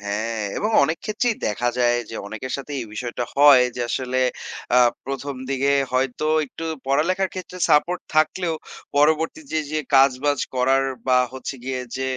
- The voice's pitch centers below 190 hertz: Yes, low, 135 Hz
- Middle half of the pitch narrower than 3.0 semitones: No, average, 3.7 semitones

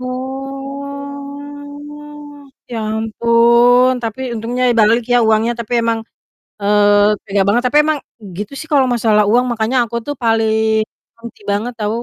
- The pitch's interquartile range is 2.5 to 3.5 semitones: No, average, 4.1 semitones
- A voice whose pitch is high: Yes, high, 240 Hz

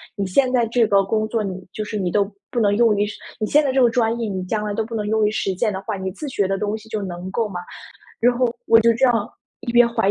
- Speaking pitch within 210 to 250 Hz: Yes, high, 215 Hz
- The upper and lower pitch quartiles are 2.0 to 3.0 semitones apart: Yes, average, 2.7 semitones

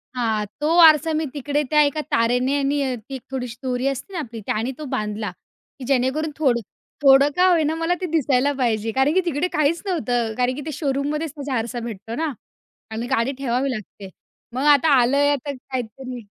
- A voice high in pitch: Yes, very high, 270 Hz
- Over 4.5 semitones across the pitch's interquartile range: No, average, 3.8 semitones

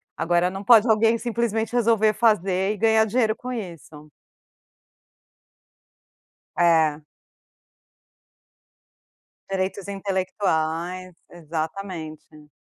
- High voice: Yes, high, 195 Hz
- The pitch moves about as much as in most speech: Yes, average, 4.6 semitones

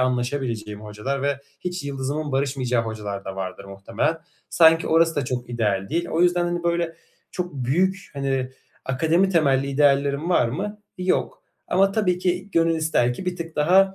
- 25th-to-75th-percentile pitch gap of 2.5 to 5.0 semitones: No, wide, 5.6 semitones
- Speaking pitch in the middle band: Yes, medium, 145 Hz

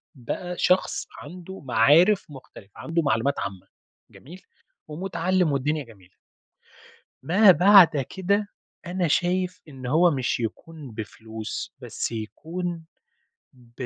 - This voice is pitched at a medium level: Yes, medium, 155 Hz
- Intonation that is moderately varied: No, wide, 6.6 semitones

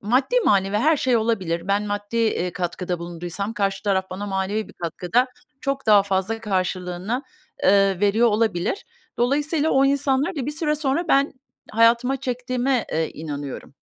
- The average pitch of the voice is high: Yes, high, 210 Hz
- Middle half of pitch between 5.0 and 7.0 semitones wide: Yes, wide, 5.6 semitones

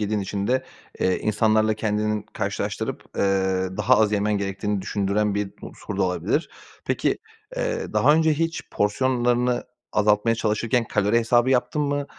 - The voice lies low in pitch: Yes, low, 105 Hz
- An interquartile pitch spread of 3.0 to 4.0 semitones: Yes, average, 3.4 semitones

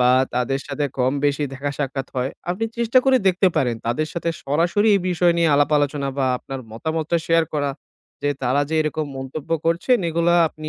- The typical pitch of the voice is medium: Yes, medium, 150 Hz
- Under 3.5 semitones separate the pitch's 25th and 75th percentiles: No, average, 3.9 semitones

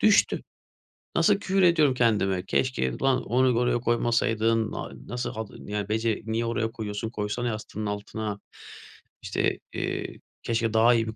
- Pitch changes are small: Yes, narrow, 2.2 semitones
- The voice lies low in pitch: Yes, low, 115 Hz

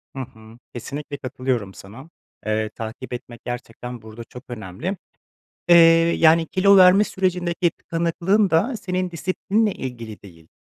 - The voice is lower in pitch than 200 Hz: Yes, low, 135 Hz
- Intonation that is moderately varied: No, wide, 8.0 semitones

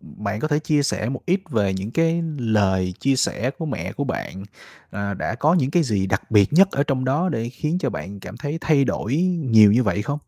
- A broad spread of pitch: Yes, wide, 6.4 semitones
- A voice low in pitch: Yes, low, 130 Hz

